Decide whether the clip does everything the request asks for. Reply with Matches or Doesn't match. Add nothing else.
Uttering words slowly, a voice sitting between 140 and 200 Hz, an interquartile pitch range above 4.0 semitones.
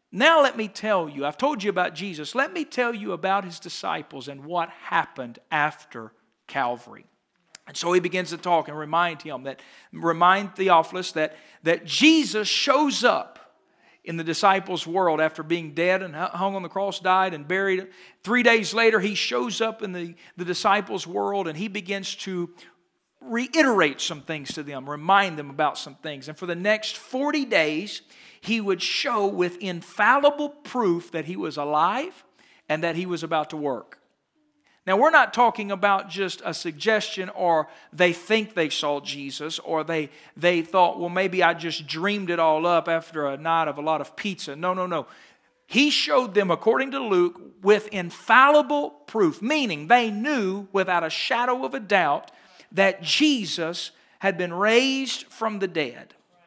Doesn't match